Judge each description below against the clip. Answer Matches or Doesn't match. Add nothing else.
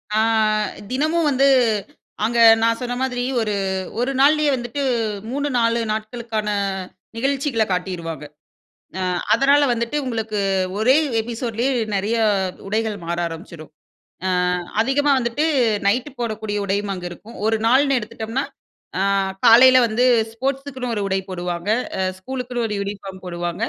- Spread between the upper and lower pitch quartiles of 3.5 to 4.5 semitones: Matches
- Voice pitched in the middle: Doesn't match